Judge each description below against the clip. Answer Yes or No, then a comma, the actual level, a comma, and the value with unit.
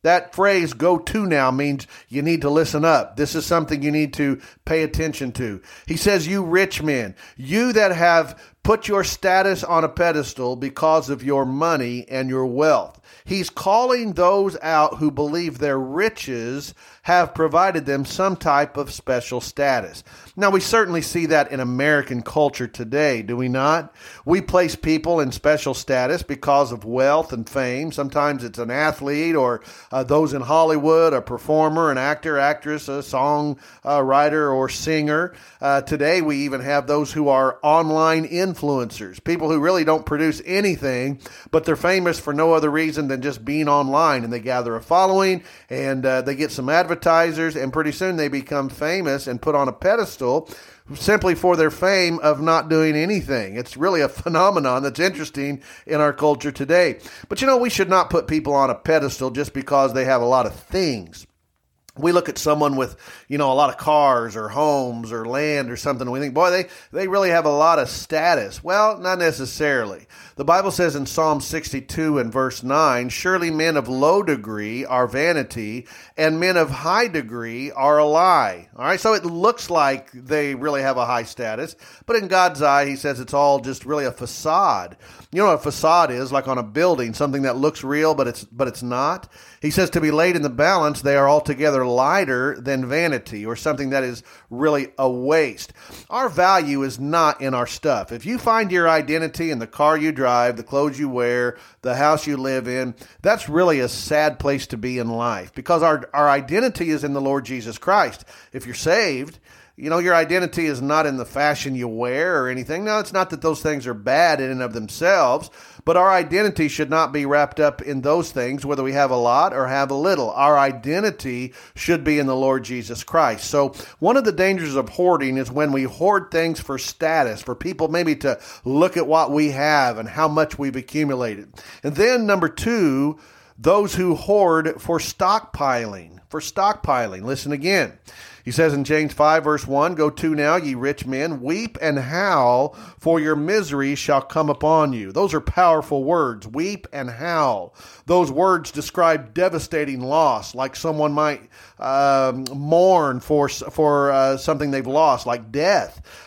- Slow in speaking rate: No, average, 190 wpm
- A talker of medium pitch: Yes, medium, 150 Hz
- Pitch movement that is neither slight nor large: Yes, average, 3.6 semitones